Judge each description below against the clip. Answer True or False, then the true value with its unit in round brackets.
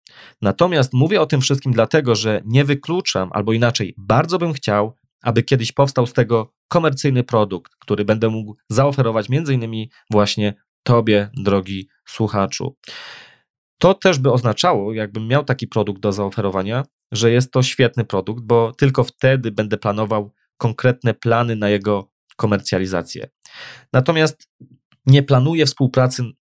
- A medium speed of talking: True (135 wpm)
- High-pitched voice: False (115 Hz)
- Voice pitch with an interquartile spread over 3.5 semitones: True (4.0 semitones)